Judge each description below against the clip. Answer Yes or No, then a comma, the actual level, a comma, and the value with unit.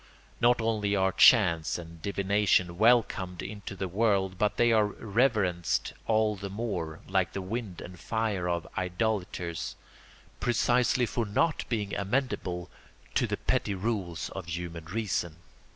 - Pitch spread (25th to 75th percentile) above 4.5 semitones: No, average, 3.8 semitones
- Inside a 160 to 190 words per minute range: No, slow, 135 wpm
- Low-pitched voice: Yes, low, 100 Hz